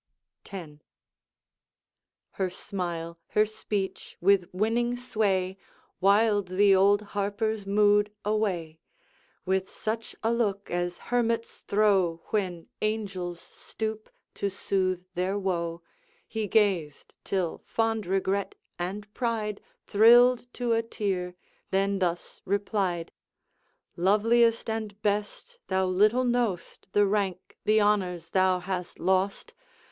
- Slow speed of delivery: Yes, slow, 110 wpm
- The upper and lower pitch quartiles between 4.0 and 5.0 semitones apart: No, average, 2.8 semitones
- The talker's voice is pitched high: Yes, high, 200 Hz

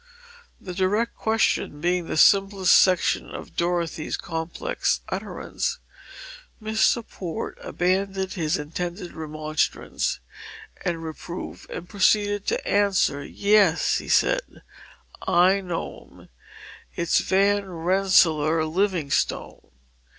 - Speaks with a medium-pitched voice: Yes, medium, 180 Hz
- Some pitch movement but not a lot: Yes, average, 3.5 semitones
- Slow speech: Yes, slow, 100 wpm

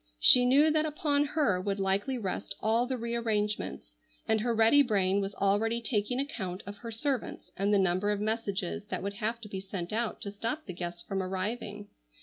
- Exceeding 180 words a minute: Yes, average, 200 wpm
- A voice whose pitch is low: No, high, 210 Hz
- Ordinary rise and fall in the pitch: Yes, average, 3.3 semitones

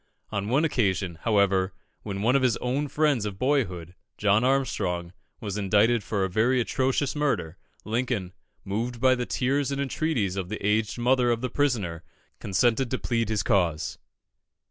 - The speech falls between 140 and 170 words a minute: Yes, average, 165 wpm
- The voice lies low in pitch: Yes, low, 115 Hz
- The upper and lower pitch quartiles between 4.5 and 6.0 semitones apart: Yes, average, 4.8 semitones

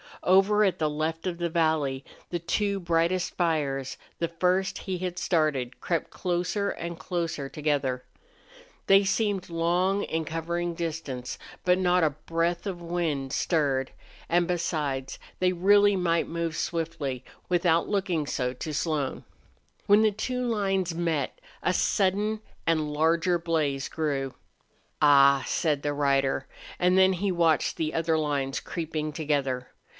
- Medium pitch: Yes, medium, 165 Hz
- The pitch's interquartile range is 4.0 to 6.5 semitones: No, average, 3.4 semitones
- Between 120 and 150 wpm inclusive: Yes, average, 140 wpm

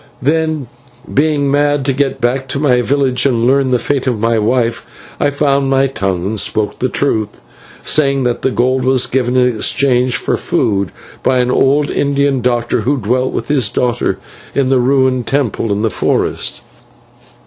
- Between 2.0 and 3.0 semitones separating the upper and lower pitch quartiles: Yes, narrow, 2.4 semitones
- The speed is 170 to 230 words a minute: Yes, average, 175 wpm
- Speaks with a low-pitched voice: Yes, low, 130 Hz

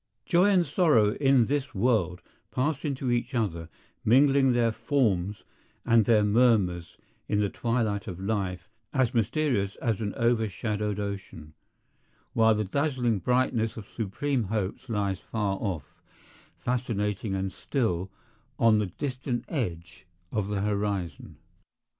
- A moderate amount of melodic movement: Yes, average, 4.3 semitones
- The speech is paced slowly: Yes, slow, 130 wpm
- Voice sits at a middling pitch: No, low, 110 Hz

